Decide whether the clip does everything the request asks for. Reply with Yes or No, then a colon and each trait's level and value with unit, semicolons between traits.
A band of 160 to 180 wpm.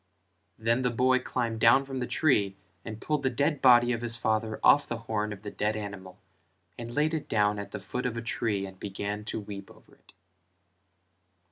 No: fast, 205 wpm